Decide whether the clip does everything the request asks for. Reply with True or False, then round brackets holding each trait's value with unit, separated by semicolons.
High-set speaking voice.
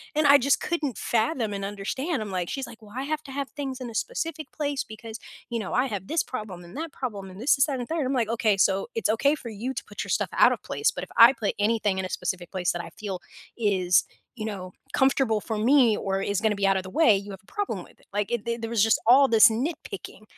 True (225 Hz)